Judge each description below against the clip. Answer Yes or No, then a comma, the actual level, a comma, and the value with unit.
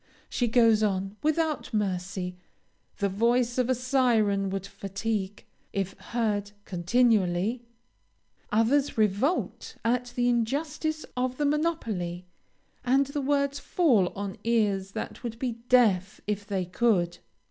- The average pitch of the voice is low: No, high, 225 Hz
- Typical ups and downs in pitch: Yes, average, 4.4 semitones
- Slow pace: Yes, slow, 125 wpm